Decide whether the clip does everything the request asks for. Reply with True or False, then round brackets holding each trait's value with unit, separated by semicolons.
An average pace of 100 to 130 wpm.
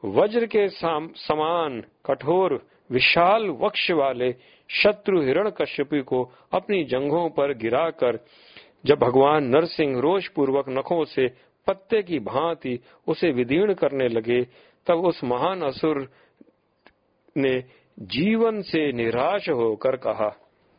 True (115 wpm)